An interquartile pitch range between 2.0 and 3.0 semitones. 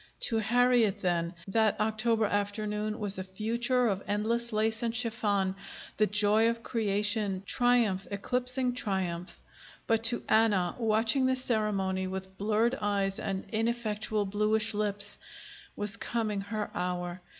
Yes: narrow, 2.5 semitones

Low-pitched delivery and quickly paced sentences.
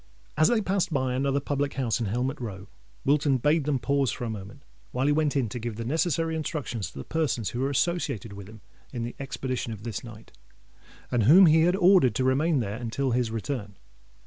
Yes: low, 130 Hz; fast, 215 wpm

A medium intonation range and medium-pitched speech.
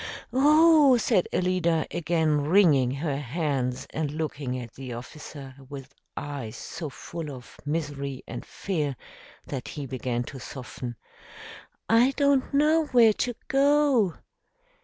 No: wide, 9.0 semitones; medium, 155 Hz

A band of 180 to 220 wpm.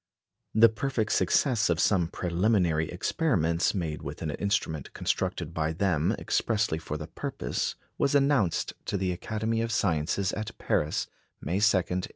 No: average, 150 wpm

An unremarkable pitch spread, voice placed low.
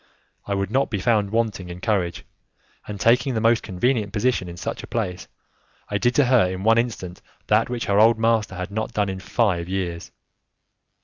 Yes: average, 3.7 semitones; low, 105 Hz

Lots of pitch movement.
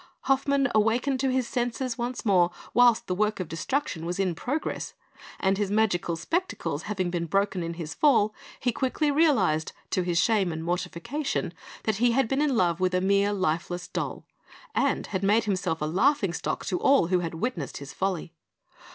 Yes: wide, 5.9 semitones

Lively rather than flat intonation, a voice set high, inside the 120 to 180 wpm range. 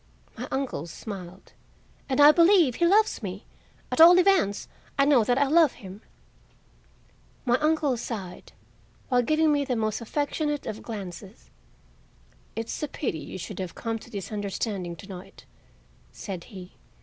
Yes: wide, 7.0 semitones; high, 235 Hz; average, 150 wpm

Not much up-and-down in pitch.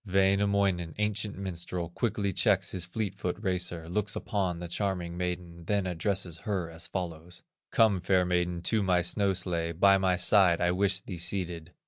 Yes: narrow, 2.2 semitones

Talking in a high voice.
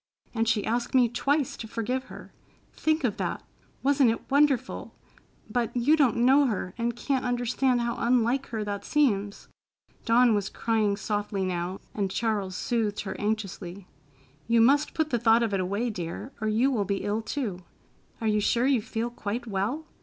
Yes: high, 230 Hz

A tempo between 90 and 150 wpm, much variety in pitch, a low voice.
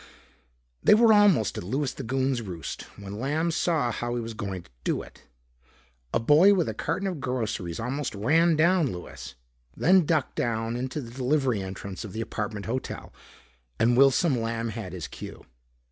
No: average, 175 wpm; wide, 5.7 semitones; low, 125 Hz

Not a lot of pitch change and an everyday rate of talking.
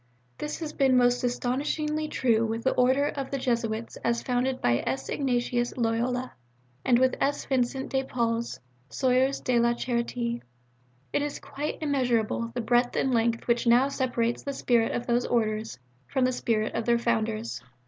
Yes: narrow, 2.0 semitones; average, 170 wpm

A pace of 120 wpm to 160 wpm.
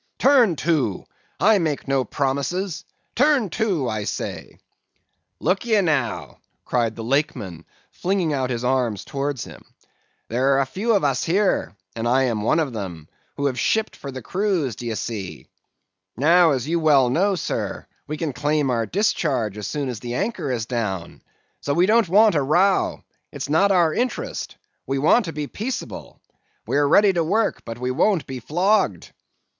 No: average, 175 wpm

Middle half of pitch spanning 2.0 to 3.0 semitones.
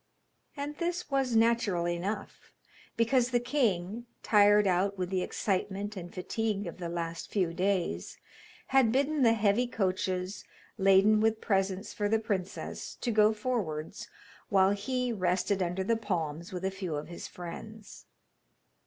No: average, 3.8 semitones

